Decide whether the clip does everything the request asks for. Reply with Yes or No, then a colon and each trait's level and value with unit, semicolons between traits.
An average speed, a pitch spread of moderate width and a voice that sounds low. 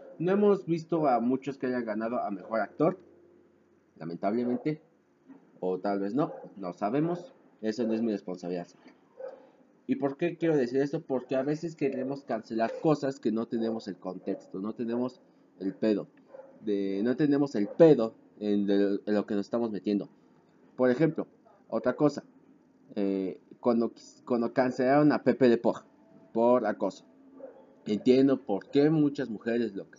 No: average, 150 wpm; wide, 5.7 semitones; low, 120 Hz